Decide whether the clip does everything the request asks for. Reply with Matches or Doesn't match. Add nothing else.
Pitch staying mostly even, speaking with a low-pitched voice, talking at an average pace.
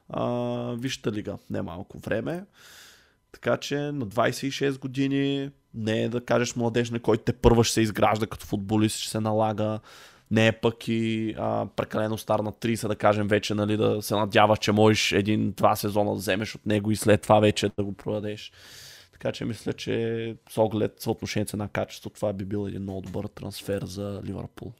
Doesn't match